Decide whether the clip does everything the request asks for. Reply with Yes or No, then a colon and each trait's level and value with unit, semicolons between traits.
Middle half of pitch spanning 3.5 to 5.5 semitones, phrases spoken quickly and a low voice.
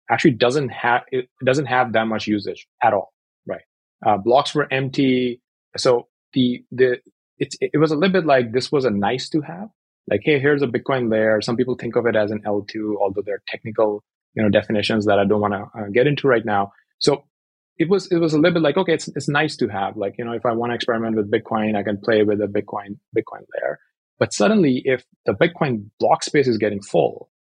Yes: average, 5.2 semitones; fast, 230 wpm; low, 120 Hz